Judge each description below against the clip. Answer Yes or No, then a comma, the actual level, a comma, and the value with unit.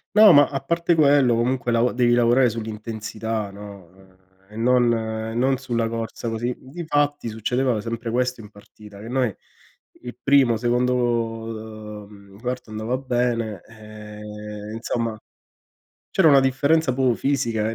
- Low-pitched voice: Yes, low, 120 Hz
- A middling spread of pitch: Yes, average, 3.0 semitones